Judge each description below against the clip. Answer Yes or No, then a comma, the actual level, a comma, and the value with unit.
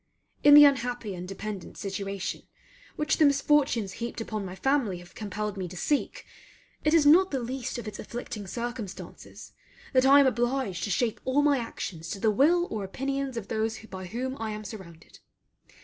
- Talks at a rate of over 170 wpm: Yes, average, 180 wpm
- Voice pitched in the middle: No, high, 230 Hz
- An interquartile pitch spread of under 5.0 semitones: No, wide, 5.4 semitones